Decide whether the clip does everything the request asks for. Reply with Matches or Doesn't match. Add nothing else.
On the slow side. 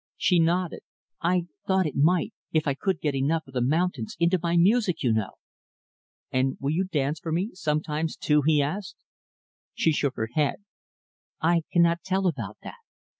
Doesn't match